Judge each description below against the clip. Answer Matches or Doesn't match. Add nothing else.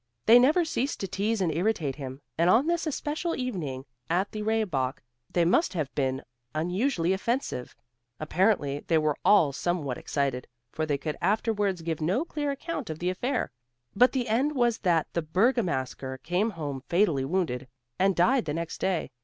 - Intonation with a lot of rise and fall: Matches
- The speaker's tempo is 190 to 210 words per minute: Doesn't match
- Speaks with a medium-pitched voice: Matches